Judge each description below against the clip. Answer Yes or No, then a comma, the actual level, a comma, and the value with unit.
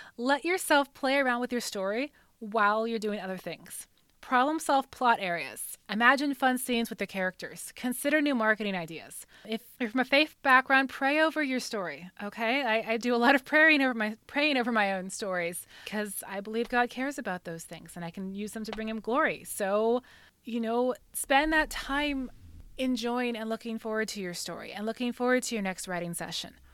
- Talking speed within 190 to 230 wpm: Yes, average, 200 wpm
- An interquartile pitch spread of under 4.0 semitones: No, average, 4.5 semitones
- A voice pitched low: No, high, 230 Hz